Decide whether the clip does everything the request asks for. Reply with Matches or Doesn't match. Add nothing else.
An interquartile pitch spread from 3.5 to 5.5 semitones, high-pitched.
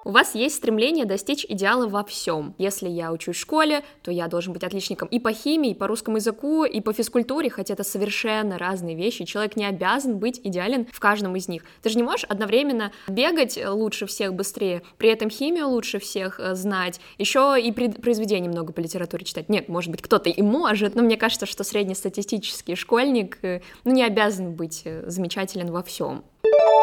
Matches